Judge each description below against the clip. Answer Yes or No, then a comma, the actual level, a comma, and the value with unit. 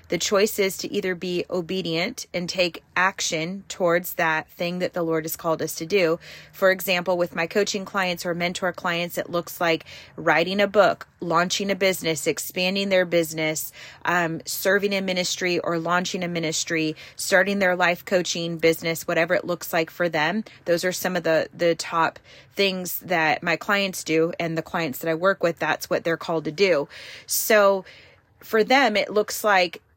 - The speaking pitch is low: No, medium, 175 Hz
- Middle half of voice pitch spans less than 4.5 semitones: Yes, narrow, 2.5 semitones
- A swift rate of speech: No, average, 185 wpm